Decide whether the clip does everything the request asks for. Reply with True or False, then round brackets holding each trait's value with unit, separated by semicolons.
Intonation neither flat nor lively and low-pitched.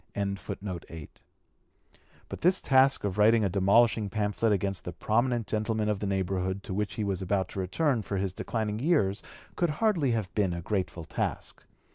True (3.1 semitones; 105 Hz)